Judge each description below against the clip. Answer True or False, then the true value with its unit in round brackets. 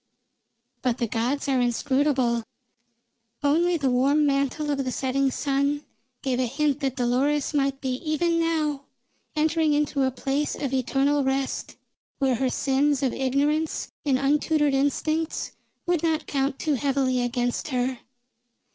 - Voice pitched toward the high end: True (275 Hz)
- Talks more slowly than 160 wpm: True (140 wpm)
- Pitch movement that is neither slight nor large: False (2.3 semitones)